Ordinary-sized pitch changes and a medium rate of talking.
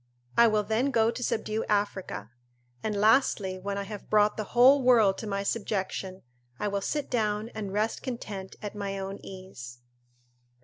No: narrow, 2.3 semitones; average, 170 wpm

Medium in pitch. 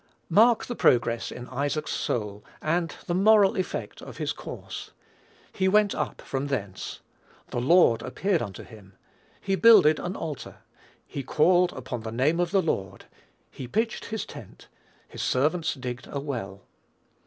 Yes: medium, 150 Hz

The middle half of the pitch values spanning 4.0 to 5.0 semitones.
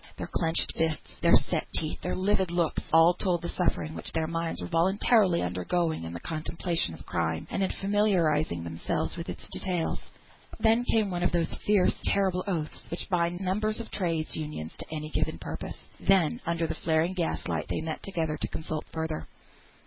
No: average, 3.0 semitones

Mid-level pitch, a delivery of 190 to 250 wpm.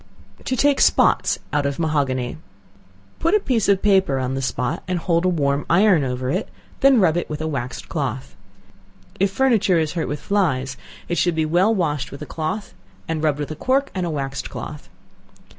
Yes: medium, 160 Hz; average, 195 wpm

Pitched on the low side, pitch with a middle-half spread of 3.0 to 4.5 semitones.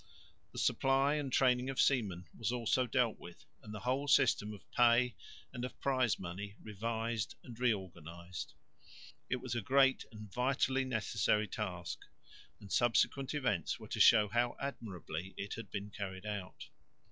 Yes: low, 115 Hz; average, 4.1 semitones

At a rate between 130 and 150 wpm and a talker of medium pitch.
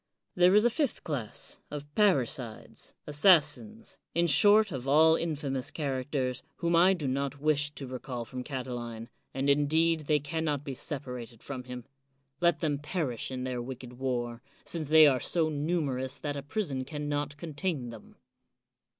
No: average, 160 wpm; medium, 145 Hz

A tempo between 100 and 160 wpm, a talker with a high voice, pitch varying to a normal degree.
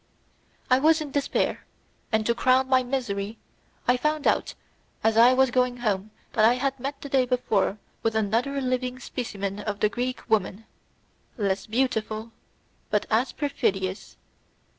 Yes: average, 150 wpm; high, 245 Hz; average, 3.3 semitones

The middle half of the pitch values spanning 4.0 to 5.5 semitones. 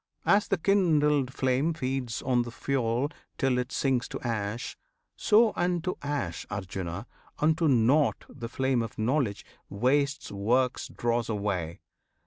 Yes: average, 4.4 semitones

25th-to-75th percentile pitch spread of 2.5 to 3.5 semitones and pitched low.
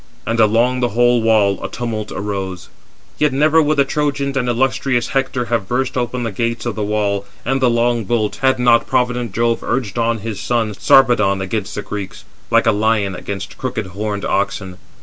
Yes: average, 3.2 semitones; low, 115 Hz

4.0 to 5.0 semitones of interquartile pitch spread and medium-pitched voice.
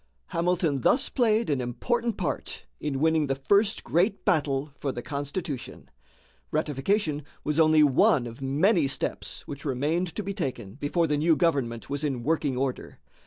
Yes: average, 4.3 semitones; medium, 150 Hz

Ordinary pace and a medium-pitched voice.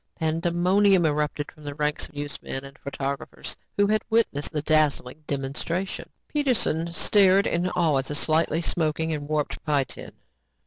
Yes: average, 150 wpm; medium, 155 Hz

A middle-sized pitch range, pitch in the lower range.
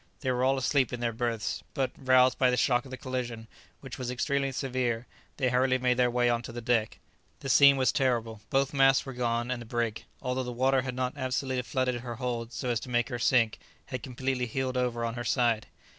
No: narrow, 1.5 semitones; low, 125 Hz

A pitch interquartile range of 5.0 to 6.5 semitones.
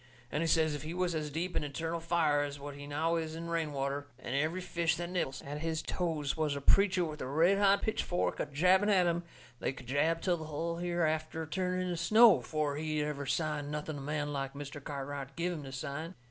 No: average, 3.0 semitones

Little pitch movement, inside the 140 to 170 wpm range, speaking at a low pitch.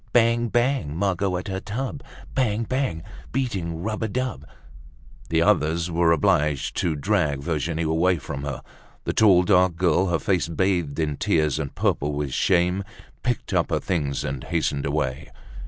No: average, 4.9 semitones; average, 160 wpm; very low, 85 Hz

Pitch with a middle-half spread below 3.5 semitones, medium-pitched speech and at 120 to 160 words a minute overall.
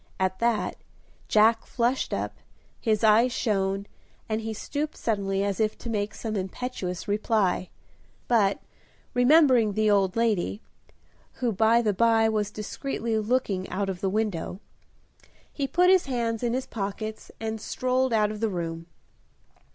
No: average, 2.8 semitones; high, 220 Hz; average, 145 wpm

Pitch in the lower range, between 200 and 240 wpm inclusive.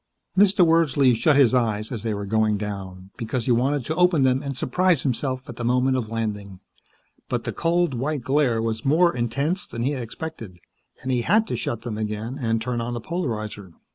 Yes: low, 125 Hz; fast, 205 wpm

